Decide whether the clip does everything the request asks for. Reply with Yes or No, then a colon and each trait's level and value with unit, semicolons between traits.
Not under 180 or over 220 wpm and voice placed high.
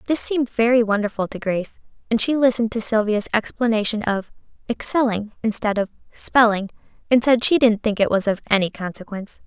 No: average, 170 wpm; high, 220 Hz